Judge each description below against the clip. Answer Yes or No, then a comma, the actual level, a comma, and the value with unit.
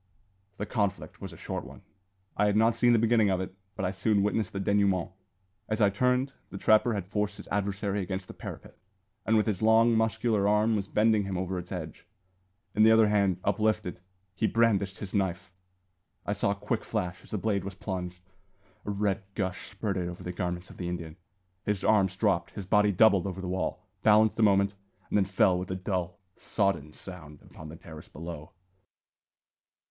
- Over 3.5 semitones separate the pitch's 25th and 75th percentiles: No, average, 2.7 semitones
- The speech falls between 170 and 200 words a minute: Yes, average, 195 wpm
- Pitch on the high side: No, low, 100 Hz